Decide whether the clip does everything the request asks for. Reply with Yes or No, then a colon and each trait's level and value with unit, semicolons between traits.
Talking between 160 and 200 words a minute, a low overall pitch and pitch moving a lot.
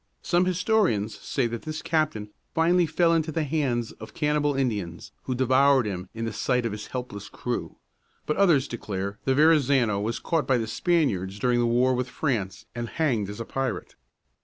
Yes: average, 185 wpm; low, 125 Hz; wide, 5.9 semitones